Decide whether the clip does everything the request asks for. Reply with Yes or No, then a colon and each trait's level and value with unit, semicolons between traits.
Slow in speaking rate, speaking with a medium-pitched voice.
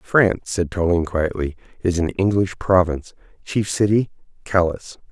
No: slow, 130 wpm; very low, 90 Hz